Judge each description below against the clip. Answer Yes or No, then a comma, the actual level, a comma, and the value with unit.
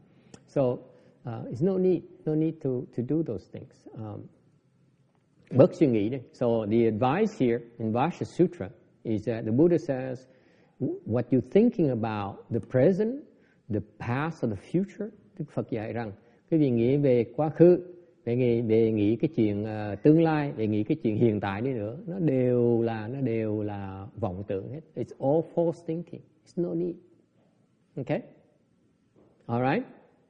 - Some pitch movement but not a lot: No, wide, 6.3 semitones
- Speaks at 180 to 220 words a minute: No, average, 170 wpm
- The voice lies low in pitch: Yes, low, 130 Hz